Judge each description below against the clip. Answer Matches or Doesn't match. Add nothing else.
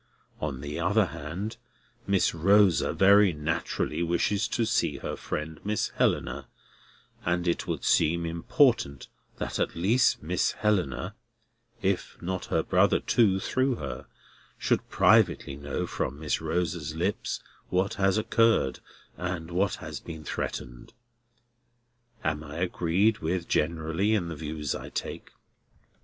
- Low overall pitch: Matches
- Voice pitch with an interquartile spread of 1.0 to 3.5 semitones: Doesn't match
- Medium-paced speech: Doesn't match